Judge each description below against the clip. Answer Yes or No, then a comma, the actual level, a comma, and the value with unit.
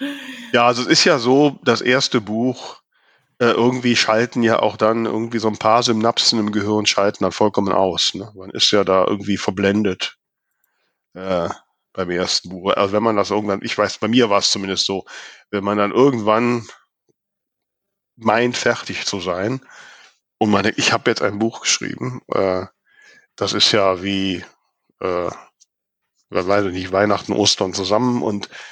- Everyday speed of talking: Yes, average, 170 wpm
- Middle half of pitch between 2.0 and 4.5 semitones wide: Yes, average, 3.2 semitones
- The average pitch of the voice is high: No, low, 105 Hz